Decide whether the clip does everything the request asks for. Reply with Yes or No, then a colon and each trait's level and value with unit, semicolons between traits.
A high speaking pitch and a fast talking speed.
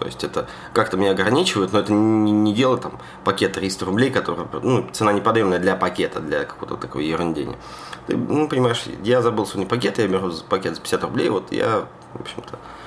No: low, 105 Hz; fast, 200 wpm